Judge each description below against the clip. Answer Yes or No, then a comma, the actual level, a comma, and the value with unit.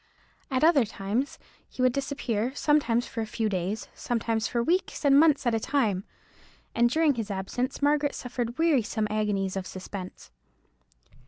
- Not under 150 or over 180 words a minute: Yes, average, 155 wpm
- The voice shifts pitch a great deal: No, average, 4.8 semitones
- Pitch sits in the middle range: No, high, 240 Hz